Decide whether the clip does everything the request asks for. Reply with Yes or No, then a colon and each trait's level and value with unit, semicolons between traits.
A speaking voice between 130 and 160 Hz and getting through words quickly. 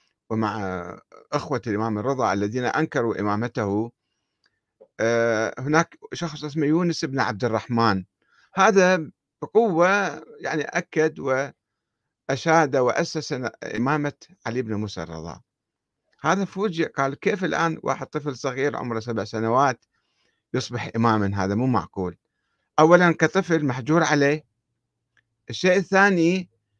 No: low, 135 Hz; average, 105 wpm